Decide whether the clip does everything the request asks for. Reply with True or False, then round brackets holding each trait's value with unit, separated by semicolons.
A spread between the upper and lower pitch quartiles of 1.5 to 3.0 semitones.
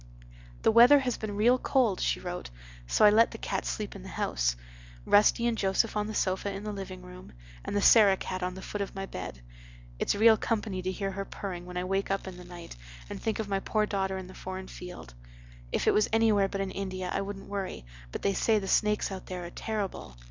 True (2.5 semitones)